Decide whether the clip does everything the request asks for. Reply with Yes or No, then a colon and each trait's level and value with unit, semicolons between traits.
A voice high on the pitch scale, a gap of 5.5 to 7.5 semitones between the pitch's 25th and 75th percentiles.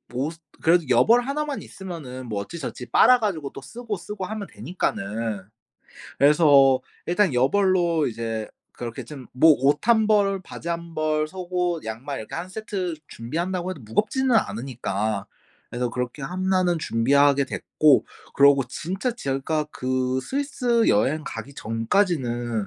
No: medium, 155 Hz; wide, 6.9 semitones